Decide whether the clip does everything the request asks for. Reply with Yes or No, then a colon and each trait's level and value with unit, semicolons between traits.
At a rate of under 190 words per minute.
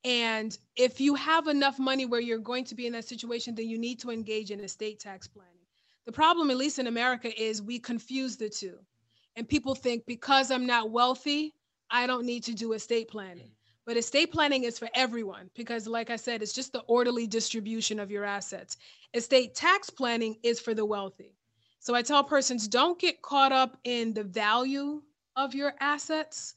No: average, 195 wpm